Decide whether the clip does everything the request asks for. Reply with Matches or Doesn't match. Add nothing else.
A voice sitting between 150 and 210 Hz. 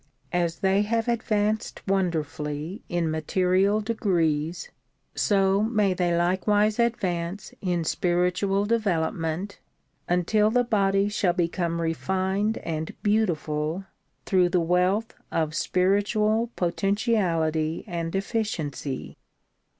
Matches